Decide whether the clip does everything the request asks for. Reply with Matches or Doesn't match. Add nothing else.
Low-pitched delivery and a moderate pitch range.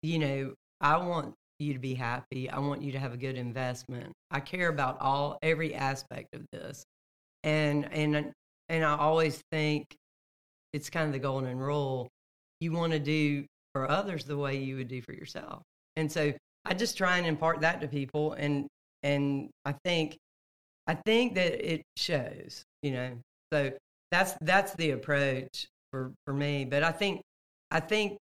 Doesn't match